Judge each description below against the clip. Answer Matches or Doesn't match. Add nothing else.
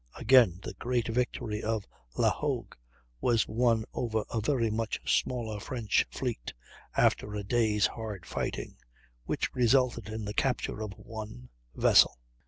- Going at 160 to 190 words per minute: Doesn't match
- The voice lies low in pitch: Matches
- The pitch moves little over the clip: Matches